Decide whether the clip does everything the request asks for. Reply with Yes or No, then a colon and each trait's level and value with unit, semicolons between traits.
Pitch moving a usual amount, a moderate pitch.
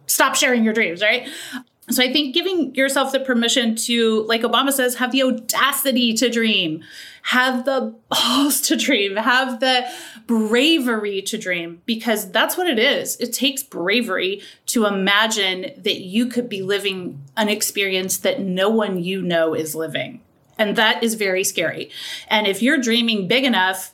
No: average, 4.6 semitones; high, 230 Hz